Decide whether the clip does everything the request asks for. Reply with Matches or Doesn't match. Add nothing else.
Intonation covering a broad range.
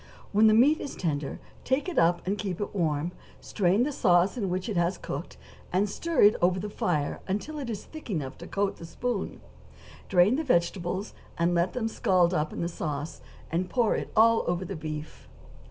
Doesn't match